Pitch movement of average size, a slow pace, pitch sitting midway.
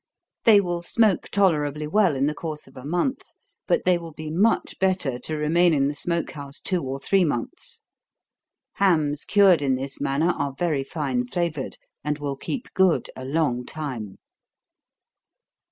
No: average, 4.2 semitones; average, 165 wpm; medium, 155 Hz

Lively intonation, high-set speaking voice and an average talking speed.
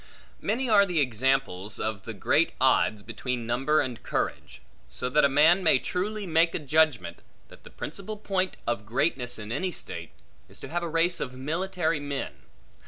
No: wide, 6.3 semitones; medium, 145 Hz; average, 175 wpm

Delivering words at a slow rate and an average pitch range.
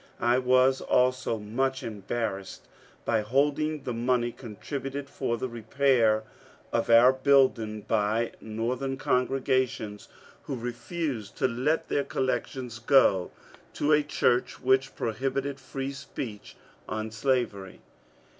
Yes: slow, 115 wpm; average, 3.0 semitones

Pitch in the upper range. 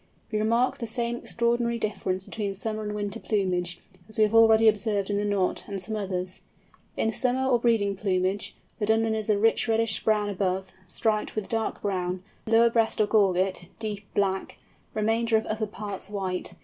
Yes: high, 210 Hz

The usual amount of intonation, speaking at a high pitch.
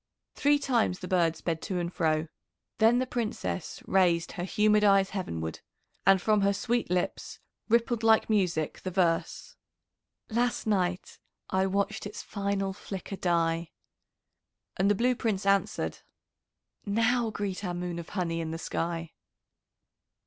Yes: average, 3.7 semitones; high, 195 Hz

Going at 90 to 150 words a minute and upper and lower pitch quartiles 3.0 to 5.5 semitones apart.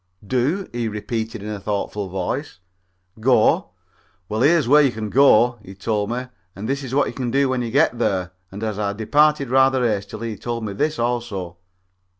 No: average, 195 wpm; average, 4.1 semitones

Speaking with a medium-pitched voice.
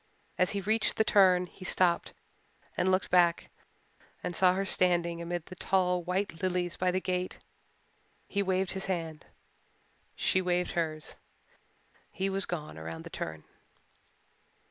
Yes: medium, 180 Hz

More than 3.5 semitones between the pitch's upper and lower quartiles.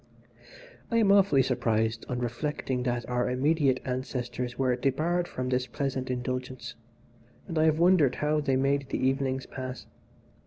No: average, 2.9 semitones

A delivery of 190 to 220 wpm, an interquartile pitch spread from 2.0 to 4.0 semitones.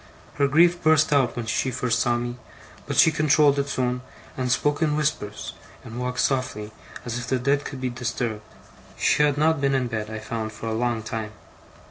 Yes: average, 200 wpm; average, 3.6 semitones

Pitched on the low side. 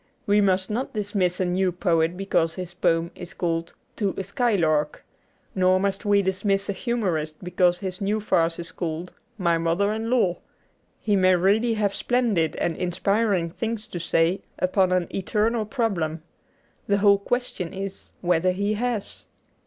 No: high, 190 Hz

